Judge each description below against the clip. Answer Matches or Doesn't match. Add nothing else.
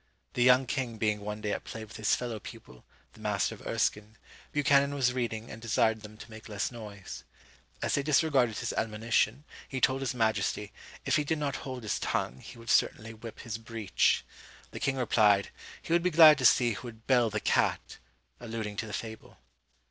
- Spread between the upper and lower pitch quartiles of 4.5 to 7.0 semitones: Doesn't match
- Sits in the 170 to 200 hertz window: Doesn't match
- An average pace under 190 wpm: Doesn't match